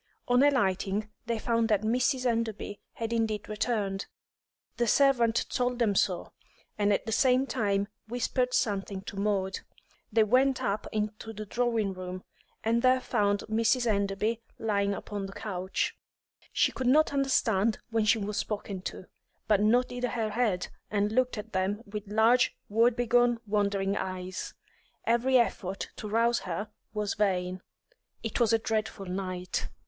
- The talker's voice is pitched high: Yes, high, 215 Hz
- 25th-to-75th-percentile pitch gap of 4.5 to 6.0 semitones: No, average, 3.0 semitones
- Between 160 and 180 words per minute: No, average, 150 wpm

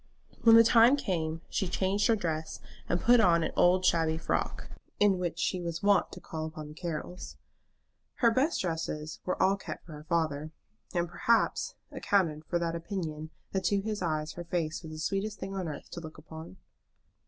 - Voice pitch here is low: No, medium, 175 Hz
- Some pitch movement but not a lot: Yes, average, 3.7 semitones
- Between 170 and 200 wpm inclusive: Yes, average, 190 wpm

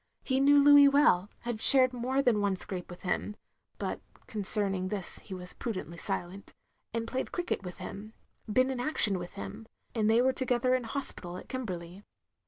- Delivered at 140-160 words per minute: No, average, 200 wpm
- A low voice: No, high, 220 Hz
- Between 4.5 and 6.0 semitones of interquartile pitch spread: Yes, wide, 5.5 semitones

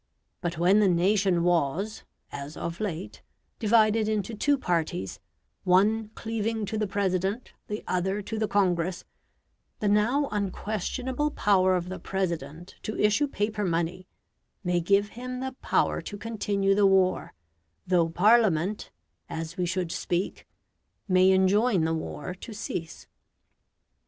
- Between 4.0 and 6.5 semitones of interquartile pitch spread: No, average, 3.3 semitones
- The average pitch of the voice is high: Yes, high, 195 Hz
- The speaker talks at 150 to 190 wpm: No, slow, 135 wpm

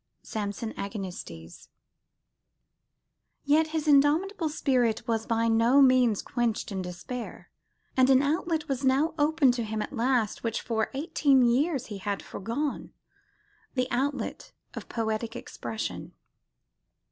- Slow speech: Yes, slow, 125 wpm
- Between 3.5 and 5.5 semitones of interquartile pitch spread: Yes, average, 4.3 semitones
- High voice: Yes, high, 245 Hz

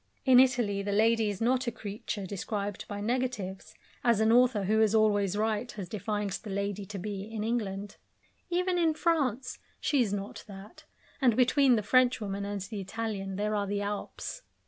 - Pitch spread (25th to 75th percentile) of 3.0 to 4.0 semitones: Yes, average, 3.3 semitones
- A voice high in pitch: Yes, high, 210 Hz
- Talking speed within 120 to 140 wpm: No, average, 180 wpm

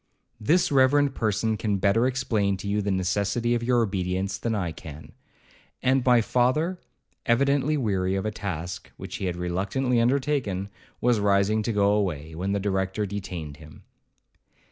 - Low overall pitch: Yes, low, 105 Hz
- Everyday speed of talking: Yes, average, 160 wpm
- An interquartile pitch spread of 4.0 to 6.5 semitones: Yes, average, 4.4 semitones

